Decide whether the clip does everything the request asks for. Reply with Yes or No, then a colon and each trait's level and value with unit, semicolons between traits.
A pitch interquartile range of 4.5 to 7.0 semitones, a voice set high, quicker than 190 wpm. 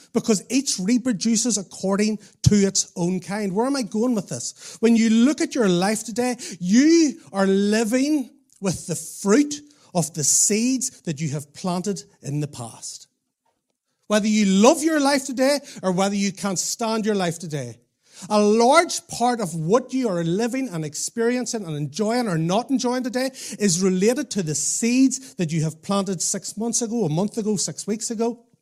No: average, 5.2 semitones; high, 210 Hz; average, 180 wpm